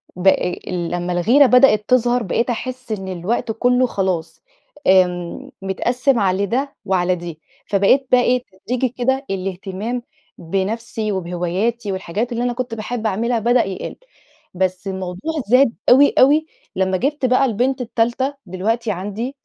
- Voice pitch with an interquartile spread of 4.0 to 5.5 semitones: Yes, average, 4.8 semitones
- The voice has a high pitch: Yes, high, 220 Hz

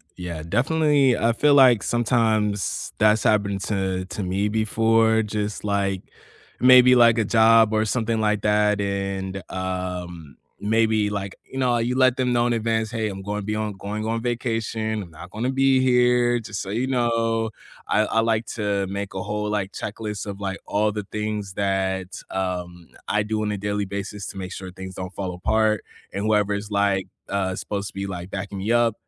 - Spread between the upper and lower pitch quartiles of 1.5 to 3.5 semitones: Yes, narrow, 2.5 semitones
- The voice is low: Yes, low, 105 Hz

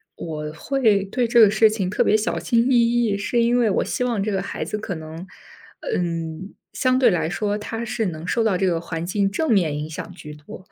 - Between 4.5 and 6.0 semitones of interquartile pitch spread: Yes, wide, 5.4 semitones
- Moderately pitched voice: No, high, 200 Hz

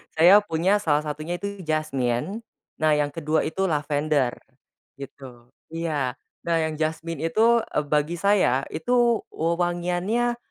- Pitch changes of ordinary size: Yes, average, 4.0 semitones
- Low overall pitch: No, medium, 160 Hz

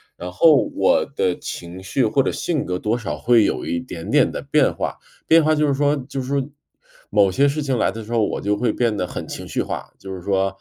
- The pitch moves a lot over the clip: Yes, wide, 6.7 semitones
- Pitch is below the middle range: Yes, low, 115 Hz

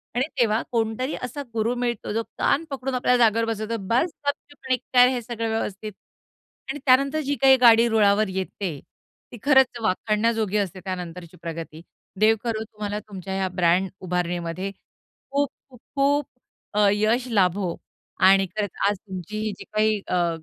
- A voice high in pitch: Yes, high, 215 Hz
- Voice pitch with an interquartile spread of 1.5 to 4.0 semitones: No, average, 4.4 semitones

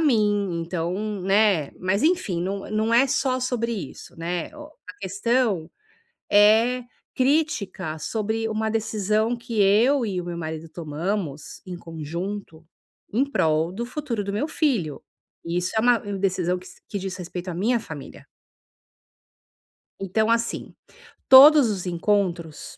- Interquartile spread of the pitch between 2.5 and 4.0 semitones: No, average, 4.8 semitones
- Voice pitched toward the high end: Yes, high, 200 Hz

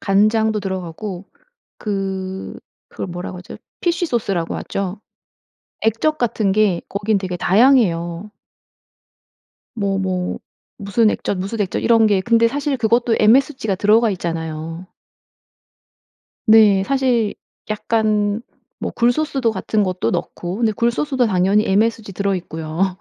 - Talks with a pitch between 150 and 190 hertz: No, high, 205 Hz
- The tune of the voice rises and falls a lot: No, average, 3.4 semitones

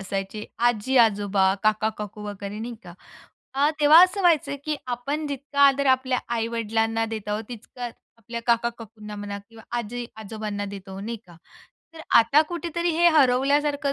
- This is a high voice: Yes, high, 230 Hz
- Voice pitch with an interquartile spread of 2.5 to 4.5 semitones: No, average, 4.9 semitones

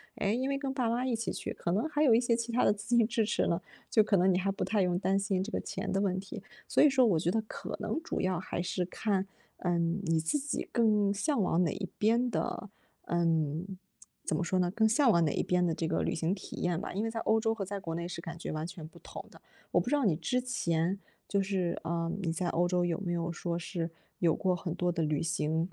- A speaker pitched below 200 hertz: Yes, medium, 185 Hz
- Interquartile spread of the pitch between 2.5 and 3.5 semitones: No, average, 4.6 semitones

